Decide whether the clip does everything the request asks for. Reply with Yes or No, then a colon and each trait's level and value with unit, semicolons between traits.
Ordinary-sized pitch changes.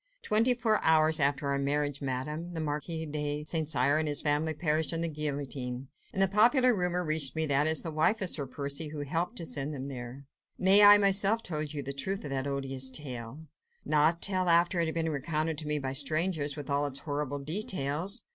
Yes: average, 3.1 semitones